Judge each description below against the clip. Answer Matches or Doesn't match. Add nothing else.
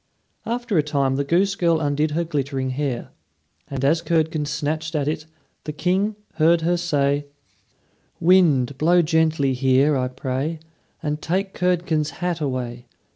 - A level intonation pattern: Doesn't match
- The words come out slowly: Doesn't match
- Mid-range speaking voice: Matches